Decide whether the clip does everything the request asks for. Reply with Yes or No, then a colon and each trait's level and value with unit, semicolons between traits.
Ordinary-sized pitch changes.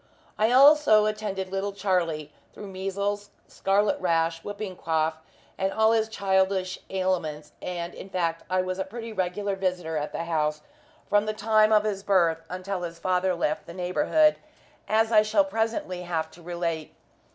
Yes: average, 3.3 semitones